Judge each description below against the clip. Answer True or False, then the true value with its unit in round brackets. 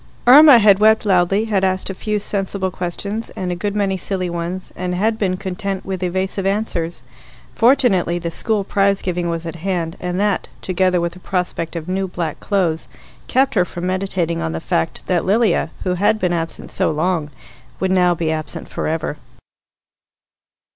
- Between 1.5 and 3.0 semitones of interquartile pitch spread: True (2.5 semitones)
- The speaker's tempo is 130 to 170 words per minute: False (180 wpm)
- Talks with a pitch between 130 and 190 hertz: True (185 Hz)